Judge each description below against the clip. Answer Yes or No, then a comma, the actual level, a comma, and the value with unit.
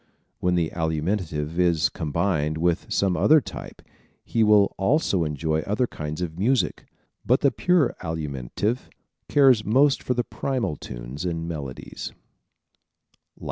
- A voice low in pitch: Yes, very low, 90 Hz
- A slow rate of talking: Yes, slow, 125 wpm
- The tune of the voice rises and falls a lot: Yes, wide, 6.6 semitones